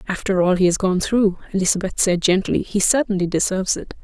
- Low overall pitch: No, high, 190 Hz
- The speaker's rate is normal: Yes, average, 195 wpm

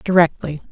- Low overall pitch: No, medium, 165 Hz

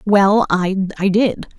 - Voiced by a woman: Yes, female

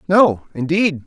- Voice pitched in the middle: Yes, medium, 165 Hz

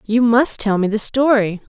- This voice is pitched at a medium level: No, high, 225 Hz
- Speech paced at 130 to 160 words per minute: No, fast, 205 wpm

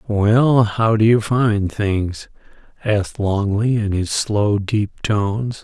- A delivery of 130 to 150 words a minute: Yes, average, 140 wpm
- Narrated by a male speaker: Yes, male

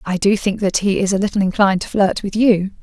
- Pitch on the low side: No, high, 195 Hz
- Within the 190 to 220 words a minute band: No, fast, 275 wpm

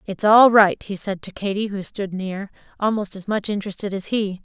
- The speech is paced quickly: Yes, fast, 215 wpm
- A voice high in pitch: Yes, high, 200 Hz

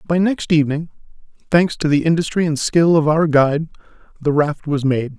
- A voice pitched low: No, medium, 155 Hz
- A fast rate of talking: No, average, 185 wpm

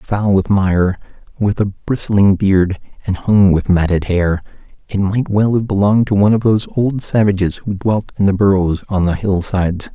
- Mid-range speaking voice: No, low, 100 Hz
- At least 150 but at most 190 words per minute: Yes, average, 185 wpm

